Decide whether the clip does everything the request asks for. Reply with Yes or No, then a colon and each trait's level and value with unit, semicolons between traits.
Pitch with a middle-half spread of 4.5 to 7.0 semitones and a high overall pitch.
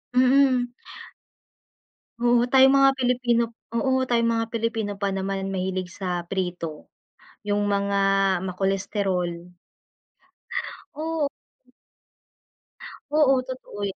Yes: average, 4.8 semitones; high, 225 Hz